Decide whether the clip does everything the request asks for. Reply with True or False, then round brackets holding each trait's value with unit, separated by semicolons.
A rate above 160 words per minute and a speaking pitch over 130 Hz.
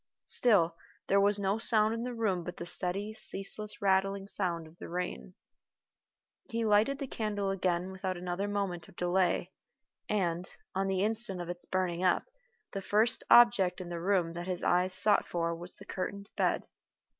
True (175 wpm; 190 Hz)